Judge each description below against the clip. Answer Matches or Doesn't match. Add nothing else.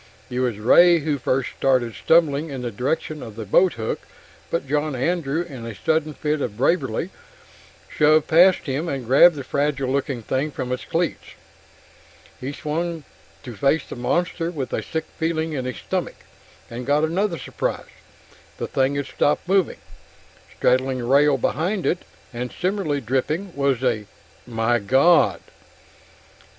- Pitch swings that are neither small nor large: Matches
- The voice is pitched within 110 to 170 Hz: Matches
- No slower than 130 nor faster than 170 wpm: Matches